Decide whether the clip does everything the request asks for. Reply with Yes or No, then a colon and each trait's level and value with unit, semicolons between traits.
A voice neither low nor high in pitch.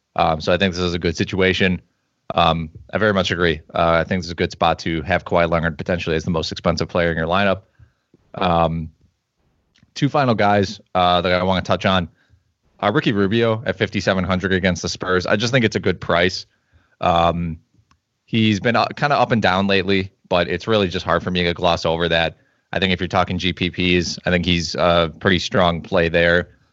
No: very low, 90 Hz